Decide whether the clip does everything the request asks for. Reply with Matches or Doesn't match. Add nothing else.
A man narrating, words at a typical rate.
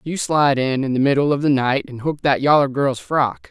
Doesn't match